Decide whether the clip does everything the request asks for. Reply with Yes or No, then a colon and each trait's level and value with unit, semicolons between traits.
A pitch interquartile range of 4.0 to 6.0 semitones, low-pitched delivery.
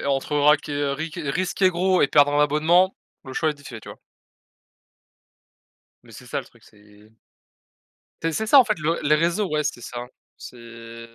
No: average, 4.4 semitones; medium, 150 Hz